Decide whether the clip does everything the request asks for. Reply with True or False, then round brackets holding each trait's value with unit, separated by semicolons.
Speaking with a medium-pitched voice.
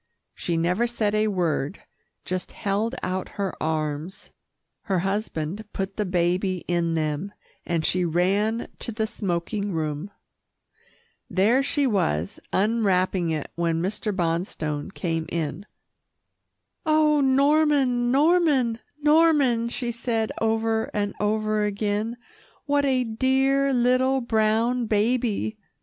False (210 Hz)